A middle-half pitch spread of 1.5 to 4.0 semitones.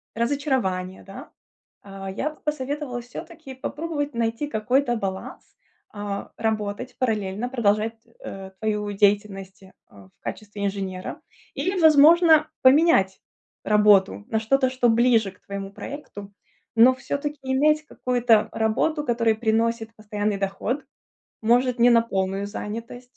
No: average, 4.5 semitones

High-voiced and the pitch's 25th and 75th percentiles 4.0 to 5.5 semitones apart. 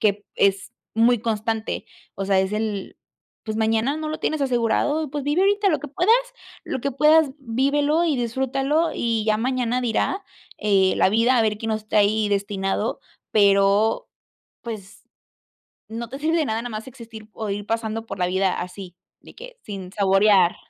Yes: high, 225 Hz; average, 4.8 semitones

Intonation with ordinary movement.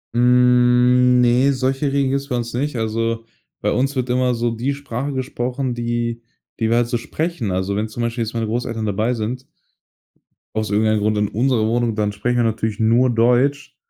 No: narrow, 2.1 semitones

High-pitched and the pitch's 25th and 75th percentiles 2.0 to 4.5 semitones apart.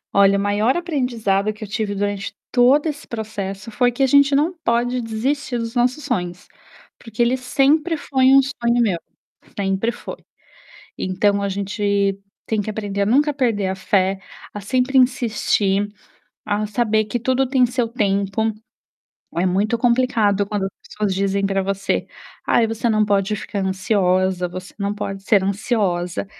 Yes: high, 215 Hz; average, 3.7 semitones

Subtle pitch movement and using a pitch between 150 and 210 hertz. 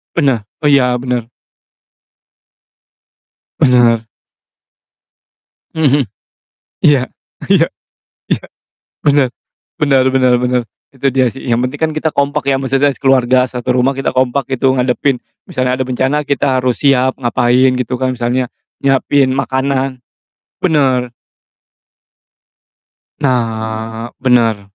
No: narrow, 1.7 semitones; low, 130 Hz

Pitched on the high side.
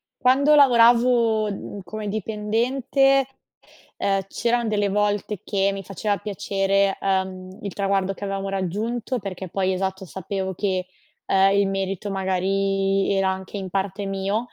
Yes: high, 195 Hz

